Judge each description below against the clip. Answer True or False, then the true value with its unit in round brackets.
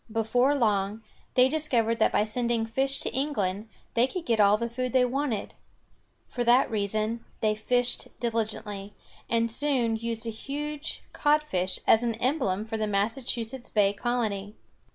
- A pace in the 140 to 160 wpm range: True (155 wpm)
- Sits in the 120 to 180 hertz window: False (230 Hz)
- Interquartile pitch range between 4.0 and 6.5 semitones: False (3.0 semitones)